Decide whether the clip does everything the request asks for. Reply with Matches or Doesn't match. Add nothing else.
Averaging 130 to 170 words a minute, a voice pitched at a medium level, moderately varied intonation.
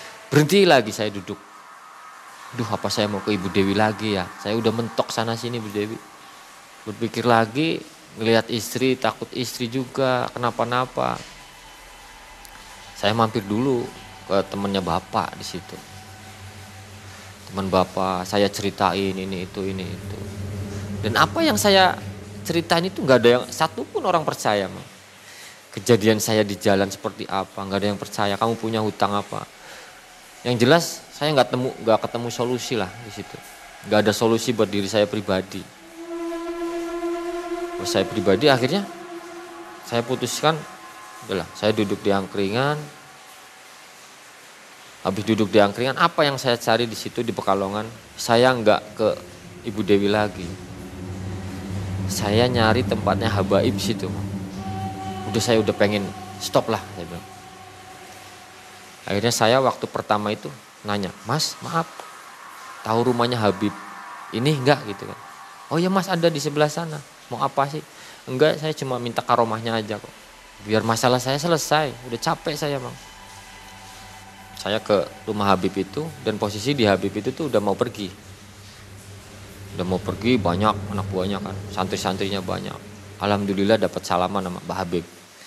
Doesn't match